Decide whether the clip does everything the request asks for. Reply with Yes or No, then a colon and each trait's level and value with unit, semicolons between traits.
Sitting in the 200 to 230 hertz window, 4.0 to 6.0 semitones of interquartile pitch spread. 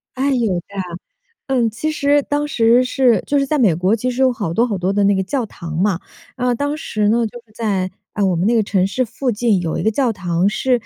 Yes: high, 225 Hz; average, 4.5 semitones